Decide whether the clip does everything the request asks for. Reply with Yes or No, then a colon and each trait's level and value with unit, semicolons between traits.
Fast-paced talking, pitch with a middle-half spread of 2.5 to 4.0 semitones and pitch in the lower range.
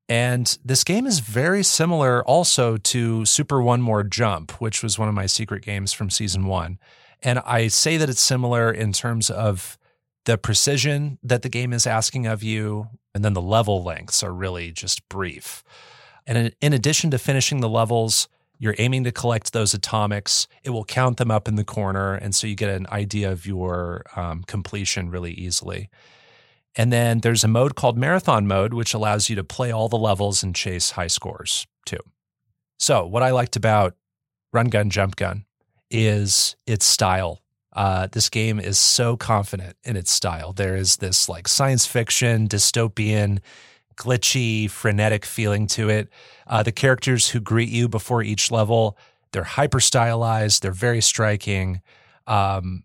No: average, 175 wpm; average, 3.3 semitones; low, 110 Hz